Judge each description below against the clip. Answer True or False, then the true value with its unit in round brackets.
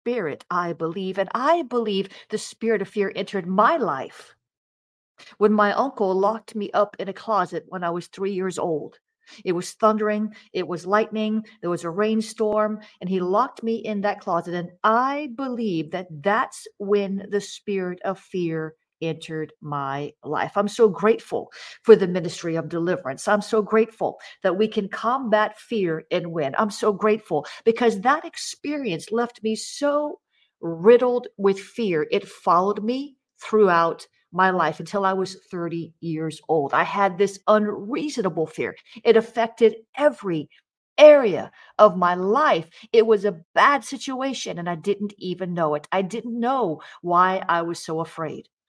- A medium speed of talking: True (160 wpm)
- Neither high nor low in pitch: False (205 Hz)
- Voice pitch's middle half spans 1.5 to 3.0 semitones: False (4.2 semitones)